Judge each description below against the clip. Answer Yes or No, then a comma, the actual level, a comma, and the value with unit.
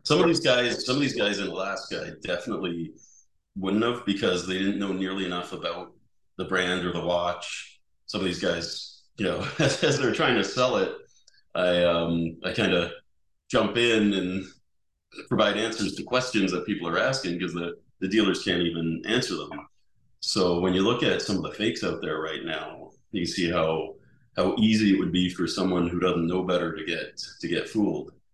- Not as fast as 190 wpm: No, average, 200 wpm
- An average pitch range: No, narrow, 2.3 semitones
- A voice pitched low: Yes, very low, 90 Hz